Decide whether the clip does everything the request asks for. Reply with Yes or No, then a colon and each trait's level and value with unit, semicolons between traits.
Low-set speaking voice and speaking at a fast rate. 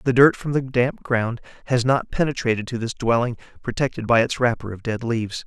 Yes: low, 120 Hz; fast, 210 wpm